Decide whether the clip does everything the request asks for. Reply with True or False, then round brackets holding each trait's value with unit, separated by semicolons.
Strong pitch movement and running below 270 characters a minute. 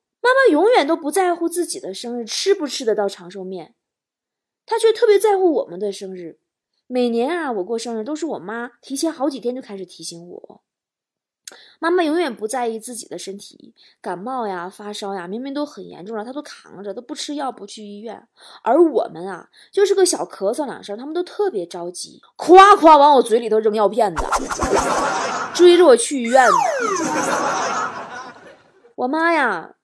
True (8.3 semitones; 260 characters per minute)